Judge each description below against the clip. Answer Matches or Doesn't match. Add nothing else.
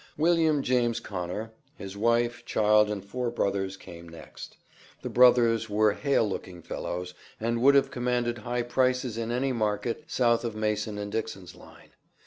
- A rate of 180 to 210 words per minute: Doesn't match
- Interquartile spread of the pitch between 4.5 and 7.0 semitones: Doesn't match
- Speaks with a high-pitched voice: Doesn't match